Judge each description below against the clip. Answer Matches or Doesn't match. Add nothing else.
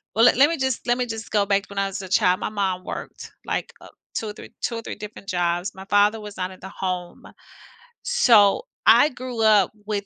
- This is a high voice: Matches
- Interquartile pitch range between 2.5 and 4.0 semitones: Matches